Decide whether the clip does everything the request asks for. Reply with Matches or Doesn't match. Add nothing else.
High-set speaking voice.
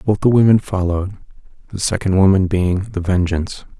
Doesn't match